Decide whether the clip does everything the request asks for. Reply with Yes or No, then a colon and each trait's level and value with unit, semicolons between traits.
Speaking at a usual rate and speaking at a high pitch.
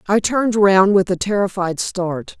Yes: average, 175 wpm; high, 195 Hz